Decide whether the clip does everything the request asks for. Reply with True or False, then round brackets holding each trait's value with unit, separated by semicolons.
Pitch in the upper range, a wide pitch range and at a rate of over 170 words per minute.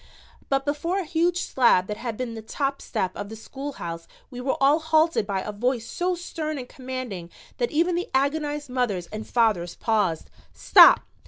True (255 Hz; 6.1 semitones; 180 wpm)